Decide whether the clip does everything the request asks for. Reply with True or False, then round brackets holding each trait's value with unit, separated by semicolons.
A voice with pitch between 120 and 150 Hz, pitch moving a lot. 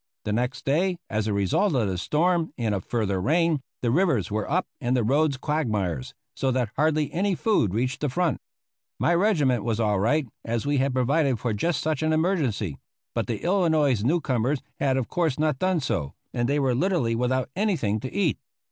True (135 Hz; 5.8 semitones)